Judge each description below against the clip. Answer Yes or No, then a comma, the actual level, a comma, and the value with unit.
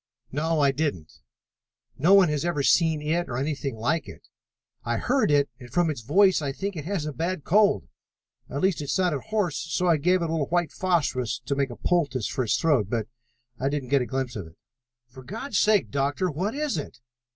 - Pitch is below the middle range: No, medium, 150 Hz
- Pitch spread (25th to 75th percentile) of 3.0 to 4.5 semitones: No, average, 4.9 semitones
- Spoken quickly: Yes, fast, 215 wpm